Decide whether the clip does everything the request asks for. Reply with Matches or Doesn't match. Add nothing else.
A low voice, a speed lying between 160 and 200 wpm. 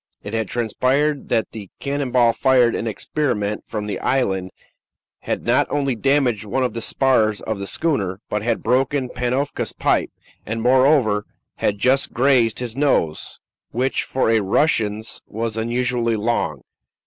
Doesn't match